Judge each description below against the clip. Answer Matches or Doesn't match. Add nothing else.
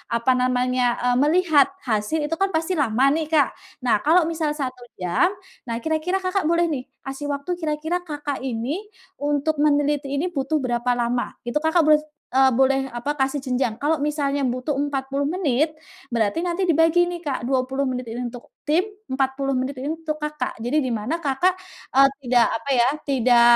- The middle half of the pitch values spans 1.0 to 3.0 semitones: Doesn't match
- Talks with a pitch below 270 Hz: Doesn't match